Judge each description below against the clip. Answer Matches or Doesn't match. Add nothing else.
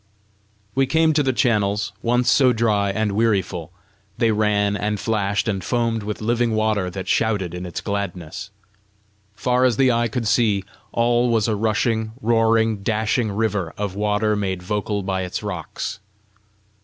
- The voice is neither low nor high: Doesn't match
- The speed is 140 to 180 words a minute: Matches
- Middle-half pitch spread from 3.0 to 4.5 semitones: Doesn't match